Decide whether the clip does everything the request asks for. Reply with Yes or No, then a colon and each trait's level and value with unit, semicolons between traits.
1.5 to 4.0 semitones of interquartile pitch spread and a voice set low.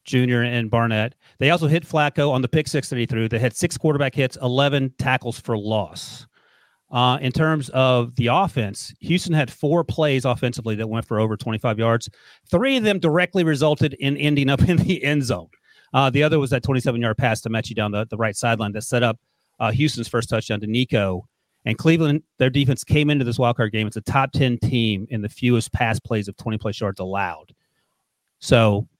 No: average, 4.4 semitones; low, 125 Hz